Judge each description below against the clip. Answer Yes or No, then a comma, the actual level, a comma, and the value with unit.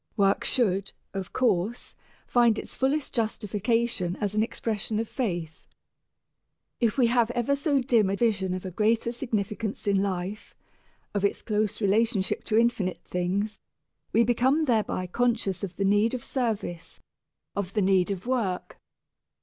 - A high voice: Yes, high, 215 Hz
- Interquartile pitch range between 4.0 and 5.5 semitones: No, average, 3.4 semitones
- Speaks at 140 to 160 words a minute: Yes, average, 150 wpm